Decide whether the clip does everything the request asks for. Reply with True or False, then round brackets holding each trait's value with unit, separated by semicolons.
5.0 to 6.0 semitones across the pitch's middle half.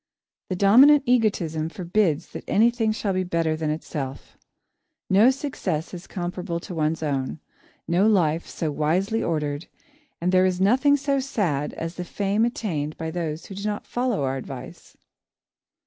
True (5.3 semitones)